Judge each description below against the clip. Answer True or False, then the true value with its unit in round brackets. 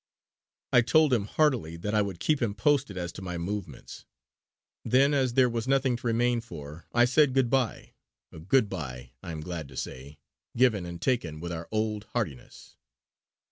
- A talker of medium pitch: False (105 Hz)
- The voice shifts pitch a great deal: True (6.9 semitones)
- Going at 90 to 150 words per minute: False (180 wpm)